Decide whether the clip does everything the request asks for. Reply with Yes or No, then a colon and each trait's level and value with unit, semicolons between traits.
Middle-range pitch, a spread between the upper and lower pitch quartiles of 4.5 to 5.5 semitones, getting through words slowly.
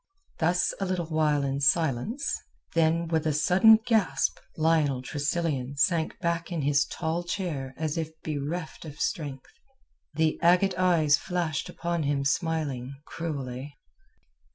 No: medium, 160 Hz; average, 3.1 semitones; slow, 130 wpm